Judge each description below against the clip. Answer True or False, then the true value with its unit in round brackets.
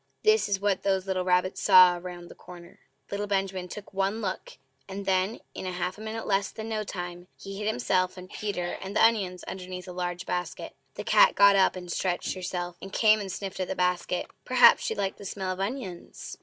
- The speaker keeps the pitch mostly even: True (1.9 semitones)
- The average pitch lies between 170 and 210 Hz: True (190 Hz)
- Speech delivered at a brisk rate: True (210 wpm)